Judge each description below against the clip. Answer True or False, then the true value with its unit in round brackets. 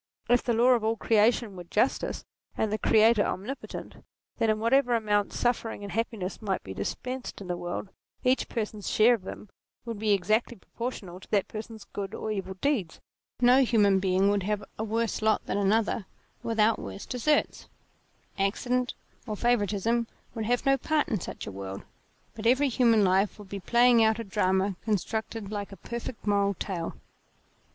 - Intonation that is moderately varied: True (3.0 semitones)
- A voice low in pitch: False (215 Hz)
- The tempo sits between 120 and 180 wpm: False (190 wpm)